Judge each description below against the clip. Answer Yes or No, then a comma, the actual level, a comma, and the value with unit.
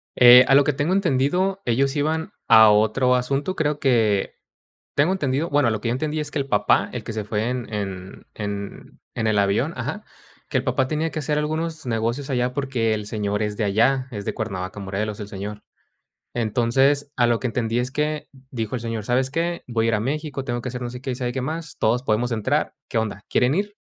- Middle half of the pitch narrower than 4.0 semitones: No, average, 4.6 semitones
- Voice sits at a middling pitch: No, low, 125 Hz